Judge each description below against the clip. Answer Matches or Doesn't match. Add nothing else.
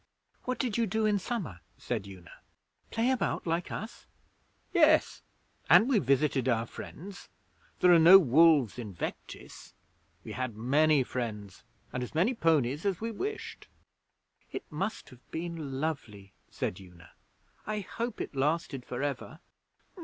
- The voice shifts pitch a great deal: Matches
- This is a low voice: Doesn't match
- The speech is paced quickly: Doesn't match